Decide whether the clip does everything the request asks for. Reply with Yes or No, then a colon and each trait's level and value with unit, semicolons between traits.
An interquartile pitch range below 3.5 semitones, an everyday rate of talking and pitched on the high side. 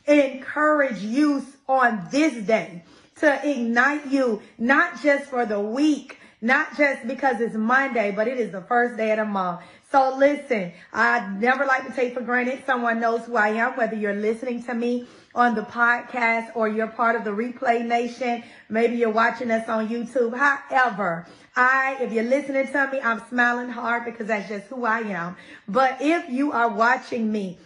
Yes: average, 2.9 semitones; average, 180 wpm; high, 240 Hz